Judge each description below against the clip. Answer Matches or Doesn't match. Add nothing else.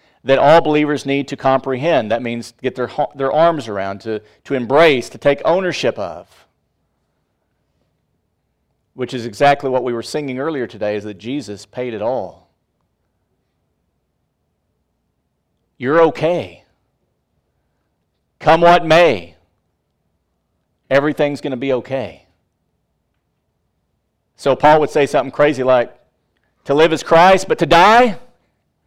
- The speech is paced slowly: Matches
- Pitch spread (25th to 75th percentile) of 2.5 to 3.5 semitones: Doesn't match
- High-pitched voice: Doesn't match